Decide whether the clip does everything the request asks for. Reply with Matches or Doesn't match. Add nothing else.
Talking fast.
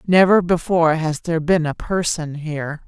Doesn't match